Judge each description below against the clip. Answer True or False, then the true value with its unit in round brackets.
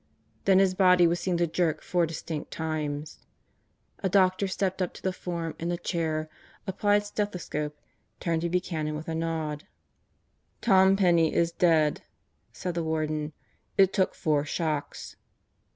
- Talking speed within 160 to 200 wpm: False (150 wpm)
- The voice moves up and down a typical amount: True (3.0 semitones)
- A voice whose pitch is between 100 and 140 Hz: False (170 Hz)